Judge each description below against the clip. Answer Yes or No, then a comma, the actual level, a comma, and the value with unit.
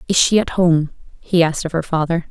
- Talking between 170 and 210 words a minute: No, fast, 235 wpm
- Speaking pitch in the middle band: Yes, medium, 165 Hz